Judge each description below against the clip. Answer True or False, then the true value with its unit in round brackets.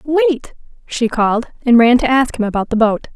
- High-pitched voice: True (245 Hz)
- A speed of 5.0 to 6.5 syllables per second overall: True (5.1 syllables/s)